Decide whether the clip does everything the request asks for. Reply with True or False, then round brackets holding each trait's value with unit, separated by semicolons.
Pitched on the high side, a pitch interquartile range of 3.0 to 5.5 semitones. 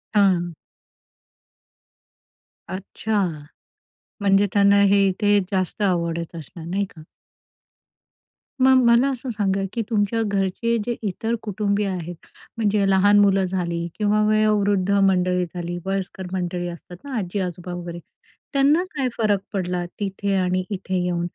False (195 Hz; 2.6 semitones)